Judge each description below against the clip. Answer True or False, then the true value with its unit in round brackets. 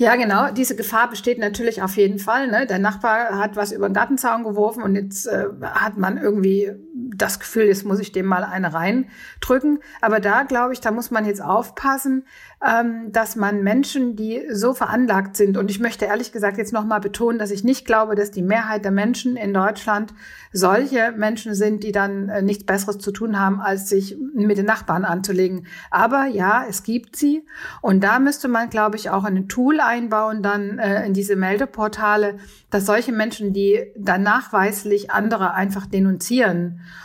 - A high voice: True (215 Hz)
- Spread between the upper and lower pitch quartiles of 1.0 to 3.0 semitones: True (2.7 semitones)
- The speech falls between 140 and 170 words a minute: False (185 wpm)